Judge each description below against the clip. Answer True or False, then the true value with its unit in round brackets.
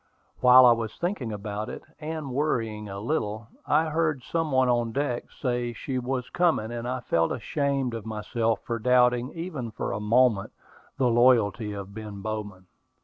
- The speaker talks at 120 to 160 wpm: False (170 wpm)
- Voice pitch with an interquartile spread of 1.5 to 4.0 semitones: True (3.5 semitones)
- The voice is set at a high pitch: False (120 Hz)